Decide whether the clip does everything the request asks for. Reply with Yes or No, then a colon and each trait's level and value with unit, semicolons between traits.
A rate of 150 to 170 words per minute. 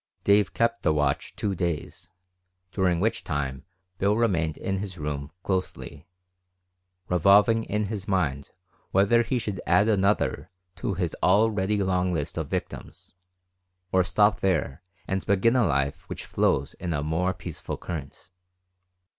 No: average, 140 wpm